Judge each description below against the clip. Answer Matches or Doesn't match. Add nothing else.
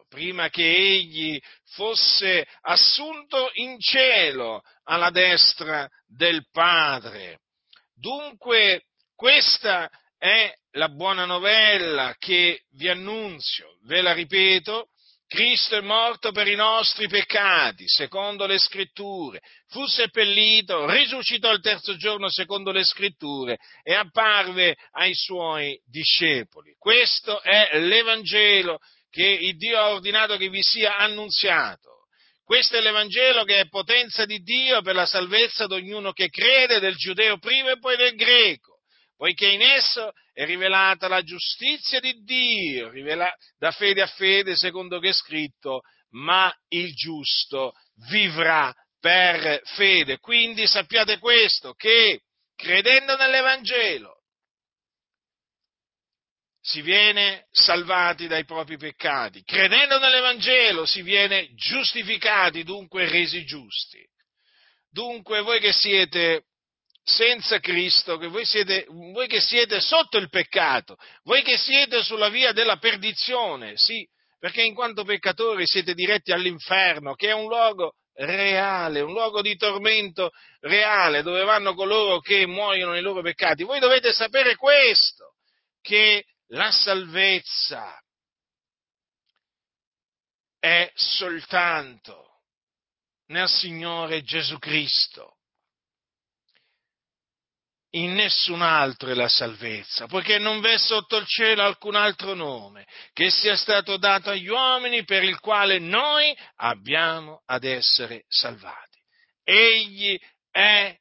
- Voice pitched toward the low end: Doesn't match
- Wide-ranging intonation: Doesn't match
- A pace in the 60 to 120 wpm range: Matches